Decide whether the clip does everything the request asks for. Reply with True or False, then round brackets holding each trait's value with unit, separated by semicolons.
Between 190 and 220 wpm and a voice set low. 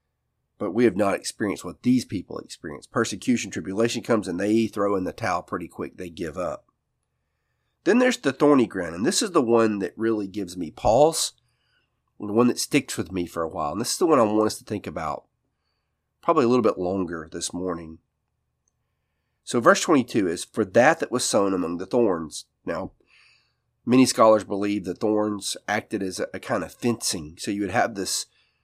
True (195 wpm; 105 Hz)